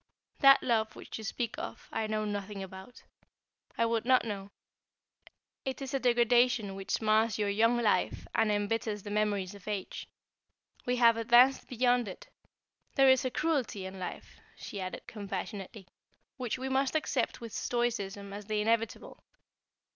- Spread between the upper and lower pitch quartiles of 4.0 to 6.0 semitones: No, average, 3.2 semitones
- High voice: Yes, high, 220 Hz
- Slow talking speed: No, average, 155 wpm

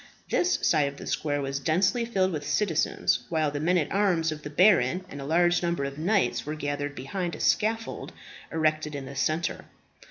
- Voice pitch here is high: No, medium, 155 Hz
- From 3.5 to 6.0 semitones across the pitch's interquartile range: Yes, average, 4.1 semitones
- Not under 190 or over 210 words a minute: Yes, average, 195 wpm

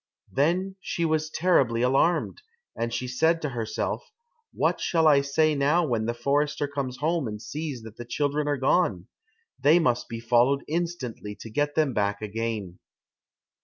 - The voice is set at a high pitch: No, medium, 140 Hz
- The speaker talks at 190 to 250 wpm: No, average, 165 wpm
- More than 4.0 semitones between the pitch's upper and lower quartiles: Yes, average, 5.1 semitones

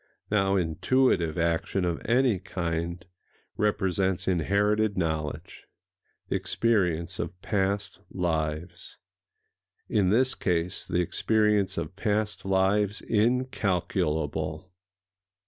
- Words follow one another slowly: Yes, slow, 85 wpm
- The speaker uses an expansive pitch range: No, average, 3.7 semitones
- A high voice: No, very low, 95 Hz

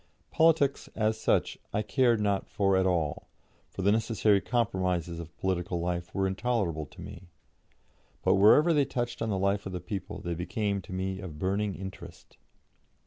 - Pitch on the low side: Yes, very low, 95 Hz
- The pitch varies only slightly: No, average, 3.2 semitones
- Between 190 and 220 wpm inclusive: No, average, 170 wpm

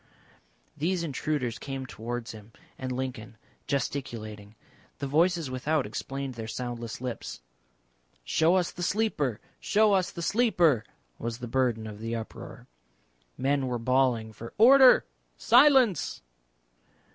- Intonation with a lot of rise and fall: Yes, wide, 6.4 semitones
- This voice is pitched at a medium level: No, low, 130 Hz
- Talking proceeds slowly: Yes, slow, 120 wpm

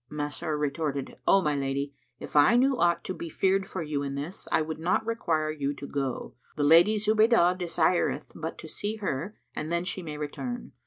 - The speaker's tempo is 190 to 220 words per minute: Yes, average, 200 wpm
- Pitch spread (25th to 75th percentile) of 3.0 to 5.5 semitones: Yes, average, 4.6 semitones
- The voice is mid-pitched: Yes, medium, 160 Hz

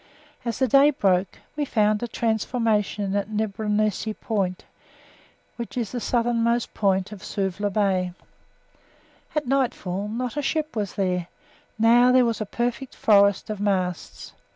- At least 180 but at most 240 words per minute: No, average, 140 wpm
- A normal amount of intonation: Yes, average, 3.3 semitones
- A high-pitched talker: Yes, high, 215 Hz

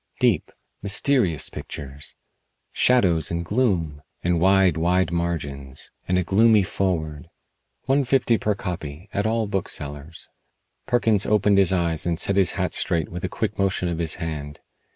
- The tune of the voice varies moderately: Yes, average, 4.0 semitones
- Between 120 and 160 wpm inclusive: Yes, average, 150 wpm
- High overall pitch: No, very low, 90 Hz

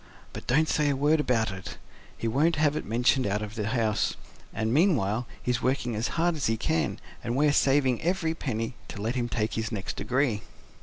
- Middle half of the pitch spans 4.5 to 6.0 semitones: Yes, average, 4.9 semitones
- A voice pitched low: Yes, low, 120 Hz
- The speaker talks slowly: No, fast, 205 wpm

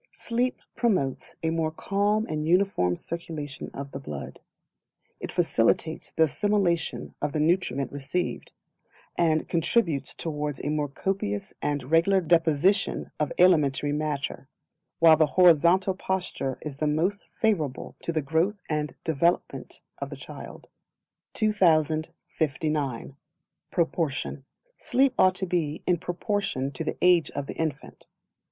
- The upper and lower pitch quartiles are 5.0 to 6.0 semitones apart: No, average, 3.7 semitones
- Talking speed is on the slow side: Yes, slow, 130 wpm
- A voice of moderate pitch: Yes, medium, 160 Hz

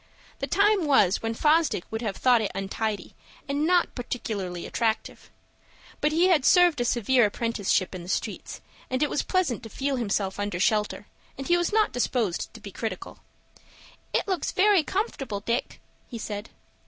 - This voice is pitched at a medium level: No, high, 245 Hz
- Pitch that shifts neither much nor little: No, wide, 7.1 semitones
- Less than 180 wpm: Yes, average, 170 wpm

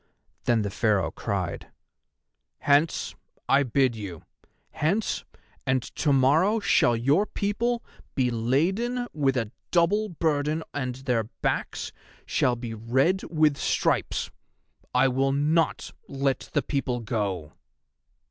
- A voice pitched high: No, low, 135 Hz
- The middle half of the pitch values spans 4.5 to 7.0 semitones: Yes, average, 5.3 semitones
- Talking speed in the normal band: No, slow, 120 wpm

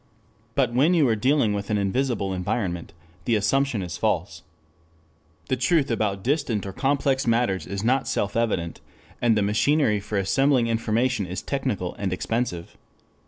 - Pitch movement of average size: Yes, average, 5.0 semitones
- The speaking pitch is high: No, low, 115 Hz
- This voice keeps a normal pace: Yes, average, 155 wpm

